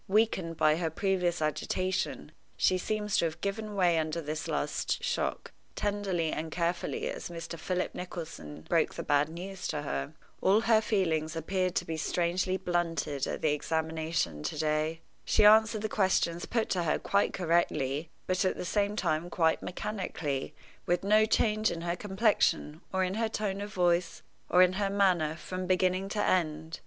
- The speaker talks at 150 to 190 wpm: Yes, average, 170 wpm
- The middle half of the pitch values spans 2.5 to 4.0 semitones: Yes, average, 3.6 semitones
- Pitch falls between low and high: Yes, medium, 180 Hz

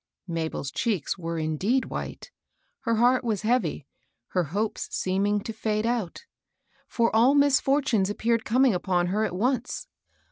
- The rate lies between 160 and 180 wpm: No, average, 140 wpm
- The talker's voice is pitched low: No, high, 215 Hz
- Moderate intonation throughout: Yes, average, 4.9 semitones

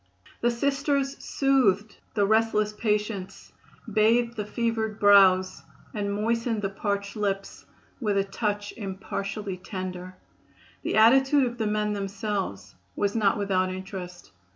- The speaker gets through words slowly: Yes, slow, 125 wpm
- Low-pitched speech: No, high, 210 Hz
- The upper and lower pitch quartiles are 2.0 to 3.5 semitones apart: Yes, narrow, 2.5 semitones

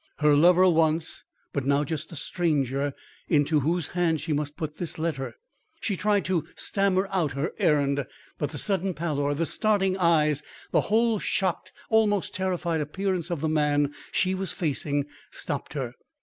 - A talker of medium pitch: Yes, medium, 165 Hz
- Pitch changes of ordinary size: Yes, average, 4.2 semitones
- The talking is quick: No, average, 165 wpm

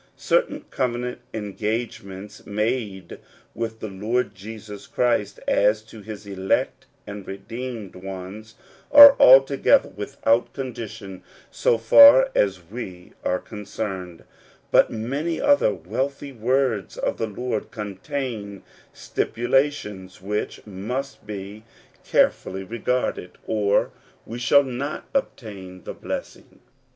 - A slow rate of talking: Yes, slow, 110 wpm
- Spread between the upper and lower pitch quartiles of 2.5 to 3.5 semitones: No, average, 4.1 semitones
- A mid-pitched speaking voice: No, low, 110 Hz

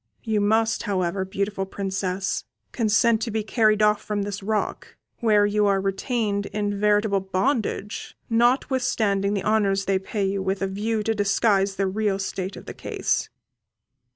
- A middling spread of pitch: No, narrow, 1.9 semitones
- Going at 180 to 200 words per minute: No, average, 155 wpm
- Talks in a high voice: Yes, high, 205 Hz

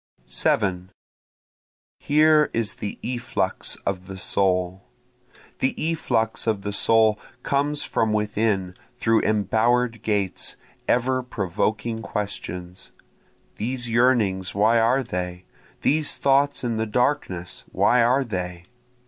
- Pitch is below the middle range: Yes, low, 110 Hz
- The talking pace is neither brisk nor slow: No, slow, 110 wpm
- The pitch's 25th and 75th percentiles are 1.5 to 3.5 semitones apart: No, average, 4.5 semitones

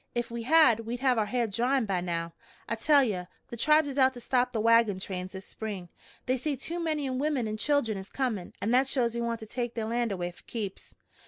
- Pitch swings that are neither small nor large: Yes, average, 3.7 semitones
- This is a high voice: Yes, high, 235 Hz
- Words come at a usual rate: No, fast, 240 wpm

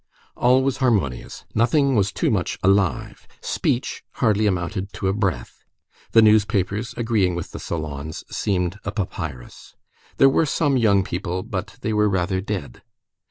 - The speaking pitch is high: No, low, 100 Hz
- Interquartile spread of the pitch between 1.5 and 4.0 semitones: Yes, average, 3.7 semitones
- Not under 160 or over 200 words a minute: No, average, 150 wpm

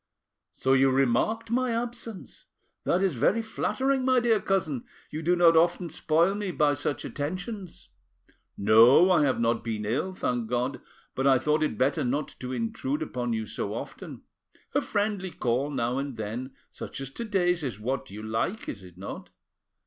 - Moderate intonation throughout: No, wide, 7.5 semitones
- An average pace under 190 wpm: Yes, average, 175 wpm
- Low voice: No, medium, 145 Hz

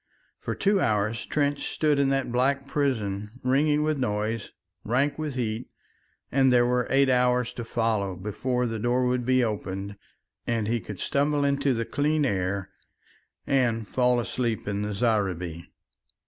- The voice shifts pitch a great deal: No, average, 4.3 semitones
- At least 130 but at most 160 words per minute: Yes, average, 155 wpm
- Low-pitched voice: Yes, low, 125 Hz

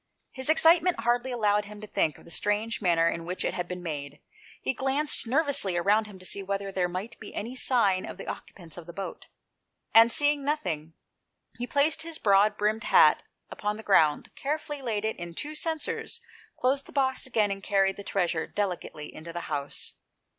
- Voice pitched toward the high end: Yes, high, 210 Hz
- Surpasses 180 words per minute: Yes, average, 195 wpm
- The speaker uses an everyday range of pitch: No, wide, 6.5 semitones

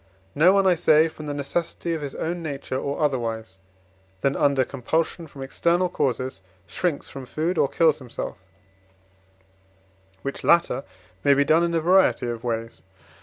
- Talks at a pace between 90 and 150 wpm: No, average, 160 wpm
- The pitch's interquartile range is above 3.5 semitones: Yes, average, 4.0 semitones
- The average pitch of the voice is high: No, medium, 145 Hz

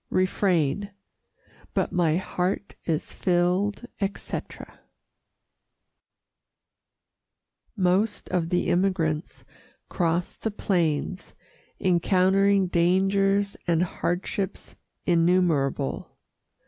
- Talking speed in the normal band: No, slow, 70 wpm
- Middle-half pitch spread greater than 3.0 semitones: No, narrow, 2.4 semitones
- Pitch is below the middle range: No, medium, 180 Hz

